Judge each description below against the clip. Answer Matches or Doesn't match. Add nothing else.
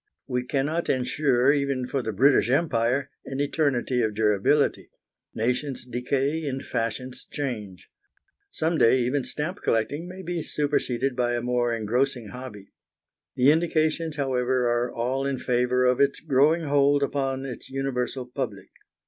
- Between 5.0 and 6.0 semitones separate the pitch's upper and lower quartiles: Doesn't match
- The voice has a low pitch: Matches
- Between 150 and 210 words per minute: Doesn't match